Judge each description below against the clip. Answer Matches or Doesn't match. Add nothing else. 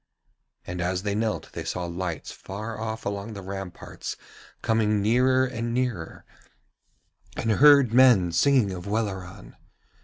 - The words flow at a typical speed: Doesn't match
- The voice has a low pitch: Matches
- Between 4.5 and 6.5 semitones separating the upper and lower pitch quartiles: Doesn't match